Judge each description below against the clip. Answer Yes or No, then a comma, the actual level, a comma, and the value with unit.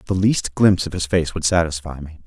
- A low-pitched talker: Yes, very low, 85 Hz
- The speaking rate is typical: No, fast, 240 wpm